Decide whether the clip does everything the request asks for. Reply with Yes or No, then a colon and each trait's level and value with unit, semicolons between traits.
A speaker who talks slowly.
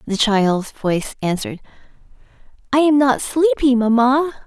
Yes: slow, 120 wpm